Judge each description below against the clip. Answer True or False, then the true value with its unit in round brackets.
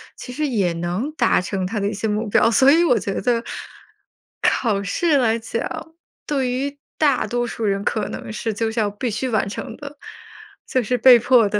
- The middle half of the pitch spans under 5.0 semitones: True (4.0 semitones)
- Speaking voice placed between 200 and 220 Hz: False (230 Hz)